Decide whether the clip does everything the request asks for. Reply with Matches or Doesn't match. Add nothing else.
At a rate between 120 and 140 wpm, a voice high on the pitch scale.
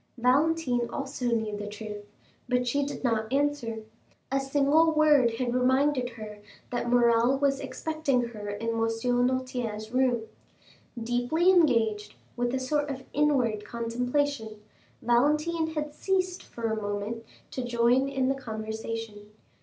Matches